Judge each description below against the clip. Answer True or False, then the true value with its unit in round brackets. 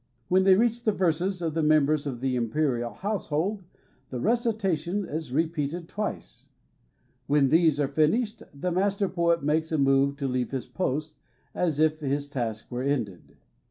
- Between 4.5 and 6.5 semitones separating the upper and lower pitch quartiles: True (4.9 semitones)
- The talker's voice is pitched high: False (155 Hz)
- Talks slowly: False (160 wpm)